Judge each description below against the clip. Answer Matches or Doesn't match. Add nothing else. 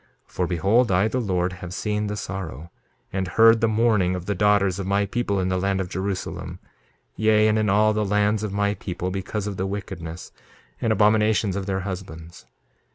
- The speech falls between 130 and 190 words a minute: Doesn't match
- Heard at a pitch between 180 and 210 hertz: Doesn't match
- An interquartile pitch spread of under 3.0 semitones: Matches